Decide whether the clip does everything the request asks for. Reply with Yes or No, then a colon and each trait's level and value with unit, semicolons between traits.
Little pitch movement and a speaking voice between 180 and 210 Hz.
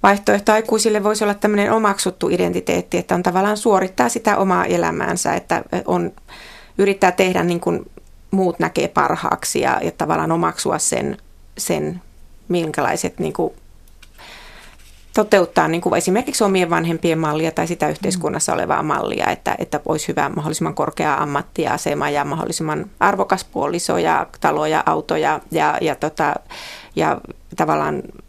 No: average, 3.3 semitones; high, 190 Hz